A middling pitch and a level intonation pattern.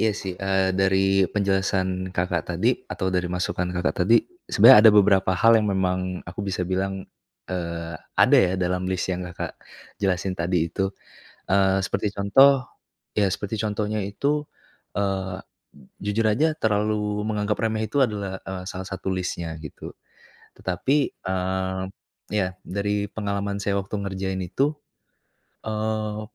No: very low, 95 Hz; narrow, 2.1 semitones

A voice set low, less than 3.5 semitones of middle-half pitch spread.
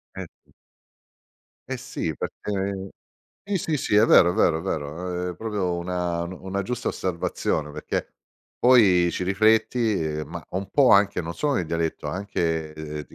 No: very low, 90 Hz; average, 3.9 semitones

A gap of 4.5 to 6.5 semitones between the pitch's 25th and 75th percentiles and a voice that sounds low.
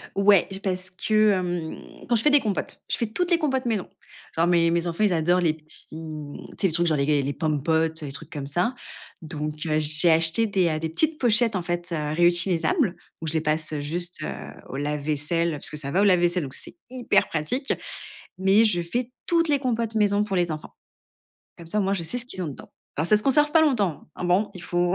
No: average, 5.1 semitones; medium, 175 Hz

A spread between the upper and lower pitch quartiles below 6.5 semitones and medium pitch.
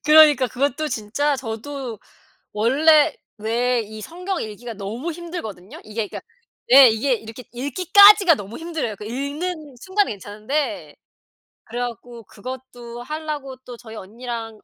No: wide, 5.4 semitones; very high, 250 Hz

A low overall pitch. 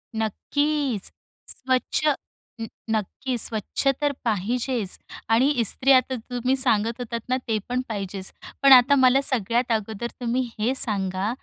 No: high, 240 Hz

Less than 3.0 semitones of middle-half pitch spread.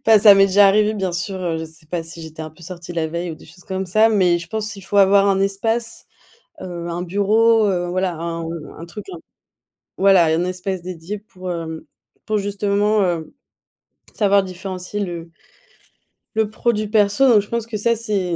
No: average, 3.3 semitones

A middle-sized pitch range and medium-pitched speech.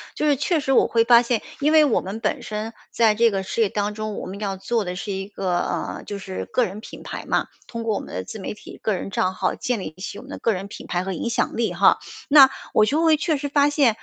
No: average, 4.4 semitones; high, 215 Hz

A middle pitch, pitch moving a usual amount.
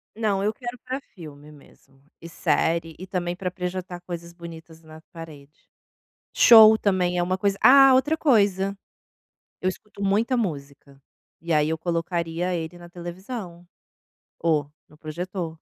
Yes: medium, 175 Hz; average, 3.4 semitones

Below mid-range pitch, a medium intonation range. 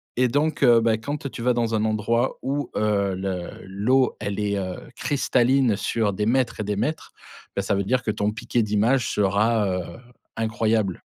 Yes: low, 110 Hz; average, 3.3 semitones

